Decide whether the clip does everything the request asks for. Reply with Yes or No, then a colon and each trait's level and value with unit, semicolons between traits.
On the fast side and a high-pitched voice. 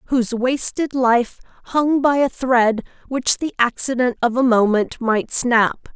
No: average, 150 wpm; high, 245 Hz